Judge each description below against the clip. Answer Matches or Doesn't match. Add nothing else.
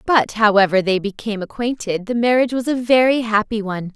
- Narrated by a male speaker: Doesn't match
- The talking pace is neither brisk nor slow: Matches